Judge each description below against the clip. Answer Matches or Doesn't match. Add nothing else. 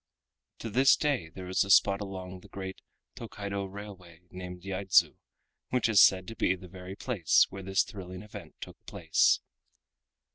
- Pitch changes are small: Matches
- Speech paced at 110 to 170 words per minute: Matches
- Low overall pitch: Matches